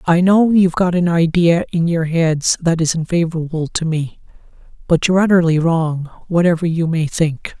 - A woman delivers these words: No, male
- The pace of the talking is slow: No, average, 175 wpm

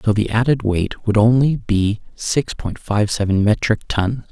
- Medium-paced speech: Yes, average, 180 wpm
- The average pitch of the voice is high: No, low, 110 Hz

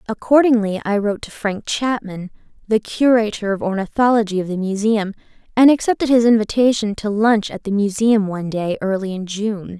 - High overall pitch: Yes, high, 210 Hz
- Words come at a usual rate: Yes, average, 165 wpm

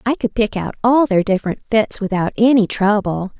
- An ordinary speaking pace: Yes, average, 195 wpm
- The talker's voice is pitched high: Yes, high, 215 Hz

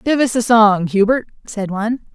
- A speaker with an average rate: Yes, average, 195 wpm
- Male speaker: No, female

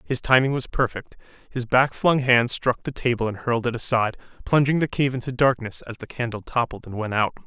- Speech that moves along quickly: Yes, fast, 215 wpm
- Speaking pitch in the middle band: No, low, 125 Hz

